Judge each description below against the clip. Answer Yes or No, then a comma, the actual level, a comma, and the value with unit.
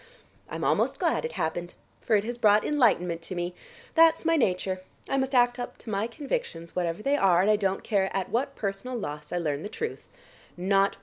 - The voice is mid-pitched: No, high, 205 Hz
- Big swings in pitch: Yes, wide, 6.0 semitones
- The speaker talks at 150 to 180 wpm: No, average, 200 wpm